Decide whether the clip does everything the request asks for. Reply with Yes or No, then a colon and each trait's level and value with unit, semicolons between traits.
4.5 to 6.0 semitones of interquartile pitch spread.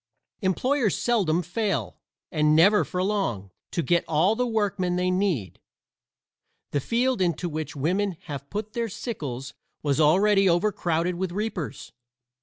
Yes: average, 5.1 semitones